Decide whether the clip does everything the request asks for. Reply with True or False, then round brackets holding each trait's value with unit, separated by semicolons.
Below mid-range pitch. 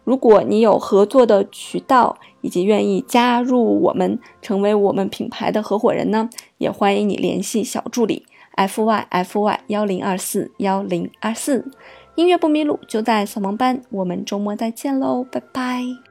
False (215 Hz)